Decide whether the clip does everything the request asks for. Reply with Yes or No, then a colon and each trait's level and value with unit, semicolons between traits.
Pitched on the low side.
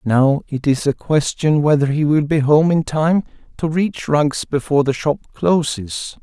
No: medium, 145 Hz